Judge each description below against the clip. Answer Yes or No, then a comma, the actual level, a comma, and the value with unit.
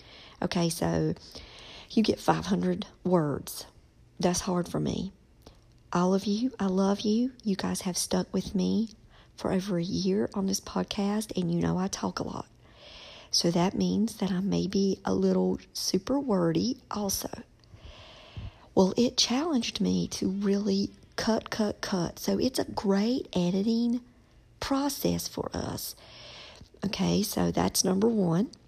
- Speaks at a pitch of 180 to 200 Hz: Yes, high, 190 Hz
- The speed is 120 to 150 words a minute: Yes, average, 145 wpm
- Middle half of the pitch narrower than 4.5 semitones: Yes, average, 3.3 semitones